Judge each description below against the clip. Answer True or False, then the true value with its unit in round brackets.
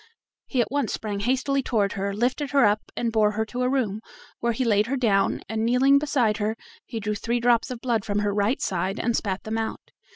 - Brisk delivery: True (230 wpm)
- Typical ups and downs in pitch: True (3.2 semitones)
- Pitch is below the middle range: False (225 Hz)